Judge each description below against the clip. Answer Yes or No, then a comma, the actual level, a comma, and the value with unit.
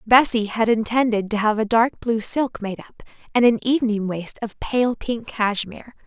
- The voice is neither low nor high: No, high, 225 Hz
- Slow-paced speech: No, average, 190 wpm